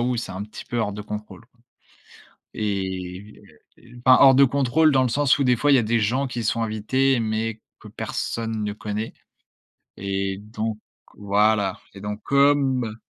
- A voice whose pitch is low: Yes, low, 110 Hz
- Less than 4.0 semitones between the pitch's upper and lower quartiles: Yes, average, 3.6 semitones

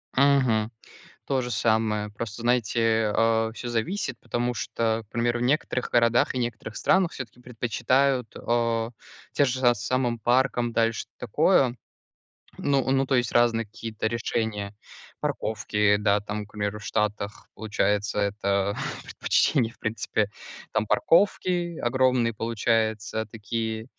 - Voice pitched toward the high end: No, low, 115 Hz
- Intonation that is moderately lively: No, narrow, 2.3 semitones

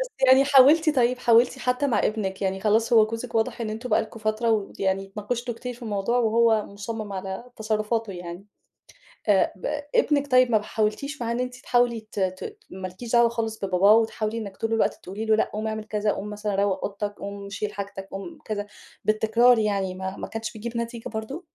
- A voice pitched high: Yes, high, 220 Hz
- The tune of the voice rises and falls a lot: No, average, 2.8 semitones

